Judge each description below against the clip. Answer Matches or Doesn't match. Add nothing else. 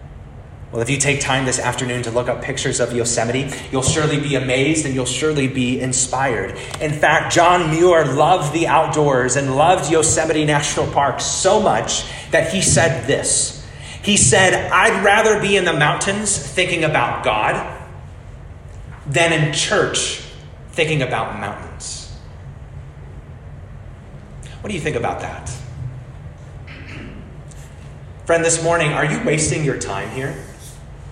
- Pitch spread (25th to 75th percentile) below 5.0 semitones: Matches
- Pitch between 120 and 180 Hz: Matches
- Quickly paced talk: Doesn't match